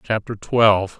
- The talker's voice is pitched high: No, low, 105 Hz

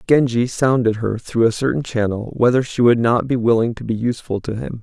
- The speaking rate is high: Yes, fast, 225 wpm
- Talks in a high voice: No, low, 115 Hz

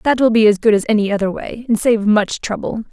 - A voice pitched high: Yes, high, 220 Hz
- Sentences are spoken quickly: Yes, fast, 265 wpm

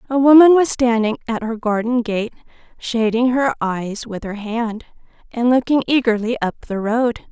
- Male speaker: No, female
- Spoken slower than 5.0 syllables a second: Yes, 4.7 syllables/s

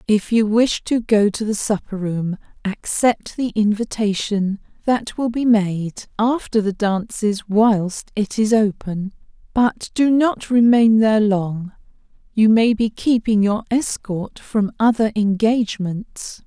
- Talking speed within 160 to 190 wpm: No, average, 140 wpm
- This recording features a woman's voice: Yes, female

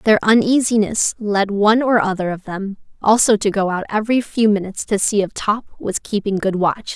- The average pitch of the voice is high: Yes, high, 205 Hz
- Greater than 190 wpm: Yes, average, 200 wpm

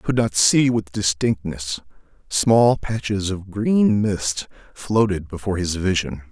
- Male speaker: Yes, male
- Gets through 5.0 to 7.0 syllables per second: No, 4.1 syllables/s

